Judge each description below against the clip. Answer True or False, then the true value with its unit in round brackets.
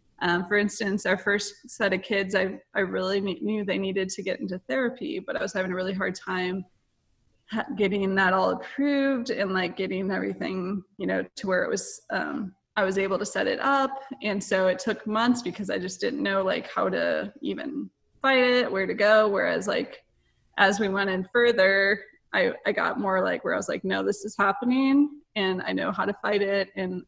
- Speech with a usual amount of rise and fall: True (3.5 semitones)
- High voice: True (200 Hz)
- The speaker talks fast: True (215 wpm)